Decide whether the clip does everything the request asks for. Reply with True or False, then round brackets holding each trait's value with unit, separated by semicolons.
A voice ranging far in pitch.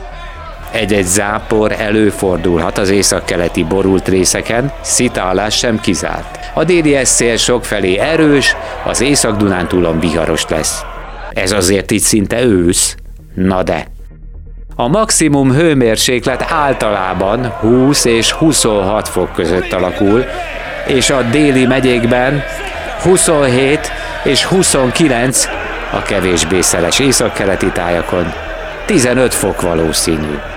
True (6.1 semitones)